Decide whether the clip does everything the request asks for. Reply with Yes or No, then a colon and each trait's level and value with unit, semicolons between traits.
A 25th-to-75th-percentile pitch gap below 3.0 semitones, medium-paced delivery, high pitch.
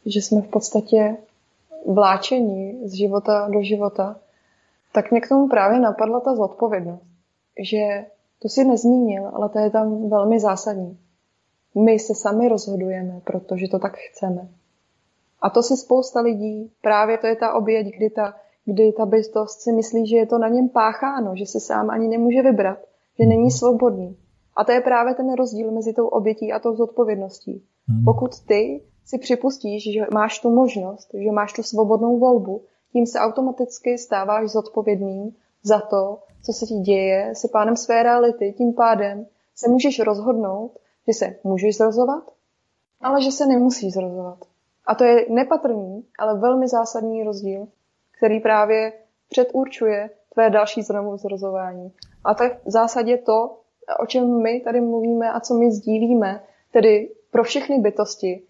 Yes: narrow, 2.5 semitones; average, 160 wpm; high, 220 Hz